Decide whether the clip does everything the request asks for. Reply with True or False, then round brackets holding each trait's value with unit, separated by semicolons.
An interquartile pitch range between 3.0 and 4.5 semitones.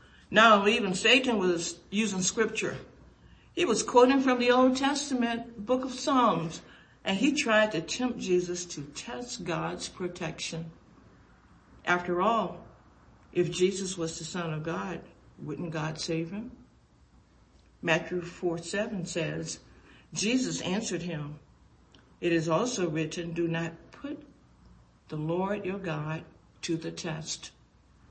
False (5.2 semitones)